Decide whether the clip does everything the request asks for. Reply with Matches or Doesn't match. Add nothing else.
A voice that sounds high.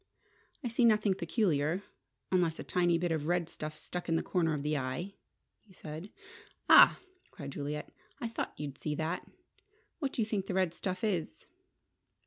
Doesn't match